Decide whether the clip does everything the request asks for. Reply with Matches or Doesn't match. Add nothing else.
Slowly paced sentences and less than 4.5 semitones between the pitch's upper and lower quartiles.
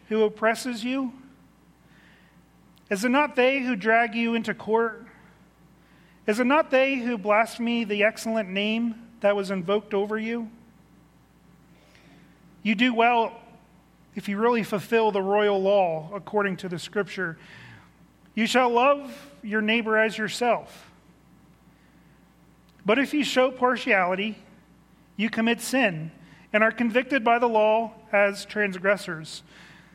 Matches